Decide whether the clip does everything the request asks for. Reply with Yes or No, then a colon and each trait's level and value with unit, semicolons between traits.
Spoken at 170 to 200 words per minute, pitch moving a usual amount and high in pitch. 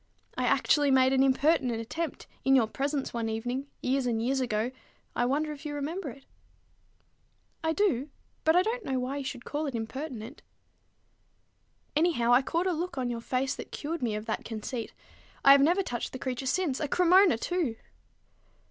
Yes: average, 185 wpm; average, 4.4 semitones; very high, 270 Hz